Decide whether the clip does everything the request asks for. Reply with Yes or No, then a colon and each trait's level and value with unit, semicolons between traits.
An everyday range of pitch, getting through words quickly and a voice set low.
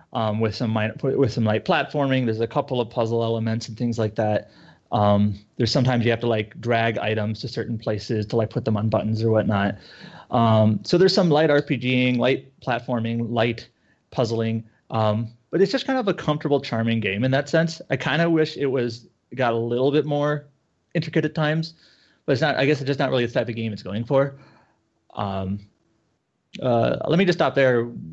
Yes: average, 4.2 semitones; fast, 210 wpm; low, 120 Hz